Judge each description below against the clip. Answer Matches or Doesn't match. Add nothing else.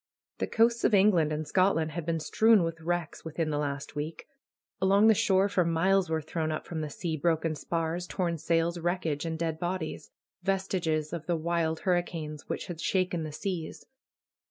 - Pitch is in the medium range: Matches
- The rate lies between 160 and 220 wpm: Matches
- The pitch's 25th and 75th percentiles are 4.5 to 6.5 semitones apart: Doesn't match